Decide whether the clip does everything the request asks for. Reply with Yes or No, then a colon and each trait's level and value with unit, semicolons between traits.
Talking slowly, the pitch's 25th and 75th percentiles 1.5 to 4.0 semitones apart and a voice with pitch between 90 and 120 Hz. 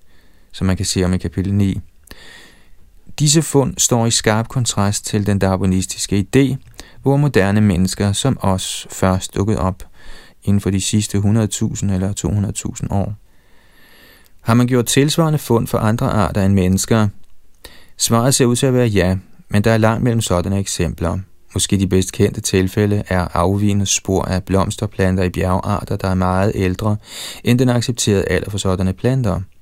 No: average, 165 wpm; average, 3.4 semitones; low, 100 Hz